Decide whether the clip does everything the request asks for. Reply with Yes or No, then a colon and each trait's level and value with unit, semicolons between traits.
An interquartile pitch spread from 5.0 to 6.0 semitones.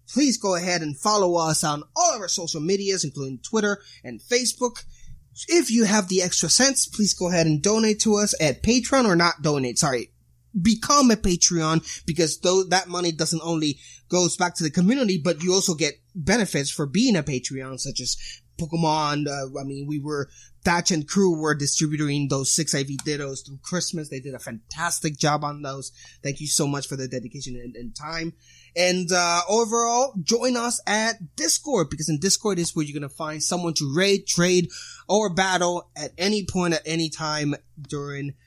No: average, 4.5 semitones